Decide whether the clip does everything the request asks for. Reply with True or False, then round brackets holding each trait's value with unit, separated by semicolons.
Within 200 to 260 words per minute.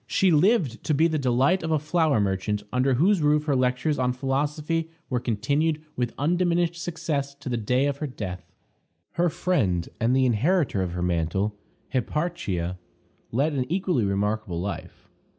False (165 wpm)